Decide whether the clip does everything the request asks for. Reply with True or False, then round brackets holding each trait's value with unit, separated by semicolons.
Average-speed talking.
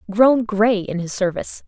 True (180 wpm)